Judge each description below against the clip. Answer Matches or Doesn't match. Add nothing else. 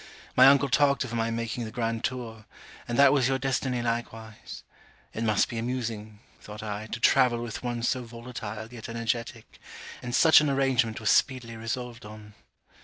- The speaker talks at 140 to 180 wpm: Matches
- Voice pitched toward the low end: Matches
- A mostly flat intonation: Matches